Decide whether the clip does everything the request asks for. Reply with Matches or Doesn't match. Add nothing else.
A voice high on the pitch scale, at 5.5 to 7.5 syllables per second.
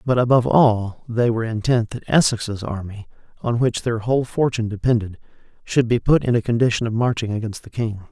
Doesn't match